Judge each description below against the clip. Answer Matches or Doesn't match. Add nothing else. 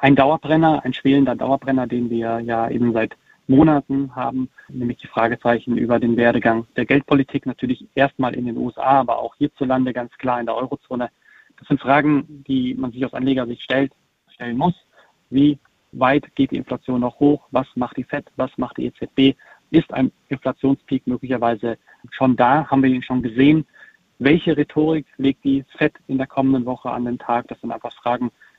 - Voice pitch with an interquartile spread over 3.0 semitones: Doesn't match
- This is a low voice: Matches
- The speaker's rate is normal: Matches